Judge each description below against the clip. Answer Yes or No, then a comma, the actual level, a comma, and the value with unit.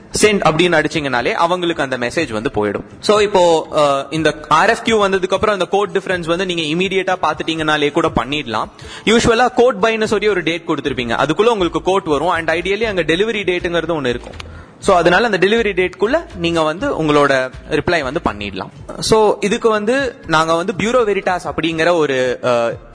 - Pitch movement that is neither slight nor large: Yes, average, 4.9 semitones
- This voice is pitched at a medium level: Yes, medium, 170 Hz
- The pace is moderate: No, fast, 165 wpm